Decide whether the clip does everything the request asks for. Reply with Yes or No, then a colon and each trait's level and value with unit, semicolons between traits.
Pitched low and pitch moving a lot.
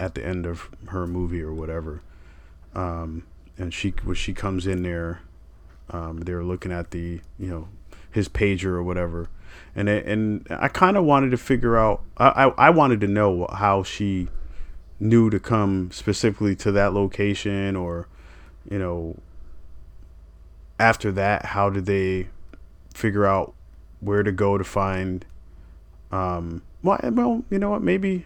No: very low, 90 Hz; average, 3.7 semitones